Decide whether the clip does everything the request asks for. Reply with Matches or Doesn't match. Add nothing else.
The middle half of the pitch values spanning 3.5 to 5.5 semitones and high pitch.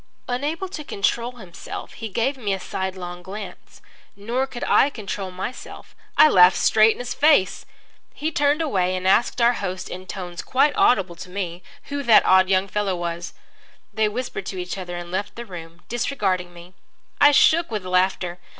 Matches